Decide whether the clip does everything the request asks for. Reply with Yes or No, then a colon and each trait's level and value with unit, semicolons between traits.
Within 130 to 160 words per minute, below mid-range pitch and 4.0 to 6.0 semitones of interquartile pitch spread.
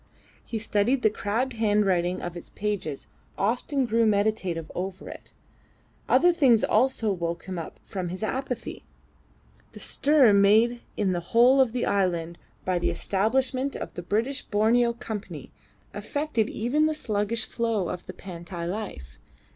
No: average, 150 wpm; high, 215 Hz; average, 4.6 semitones